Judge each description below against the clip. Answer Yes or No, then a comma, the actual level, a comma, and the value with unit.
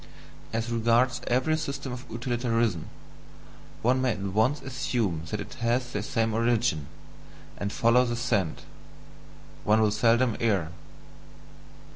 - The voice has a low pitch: Yes, low, 115 Hz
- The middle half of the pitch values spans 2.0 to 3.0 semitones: Yes, average, 2.7 semitones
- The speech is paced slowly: Yes, slow, 125 wpm